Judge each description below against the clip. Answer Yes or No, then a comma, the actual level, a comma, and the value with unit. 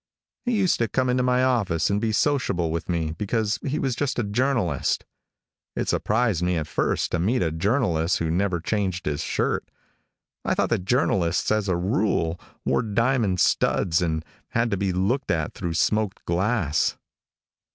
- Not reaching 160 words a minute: No, average, 170 wpm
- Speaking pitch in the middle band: No, low, 100 Hz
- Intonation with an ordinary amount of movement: No, wide, 5.8 semitones